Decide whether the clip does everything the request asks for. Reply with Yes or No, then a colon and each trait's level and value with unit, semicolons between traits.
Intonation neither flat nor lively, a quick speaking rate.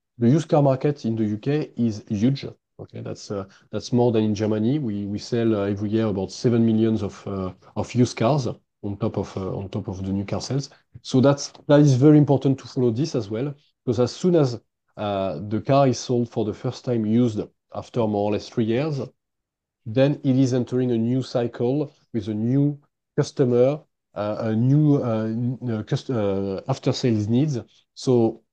Yes: average, 3.9 semitones; fast, 200 wpm